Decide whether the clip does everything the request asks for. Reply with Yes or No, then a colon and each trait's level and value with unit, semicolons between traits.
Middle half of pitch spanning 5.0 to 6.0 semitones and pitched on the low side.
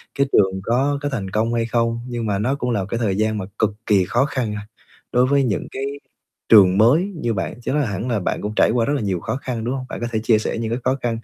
No: average, 3.2 semitones; low, 115 Hz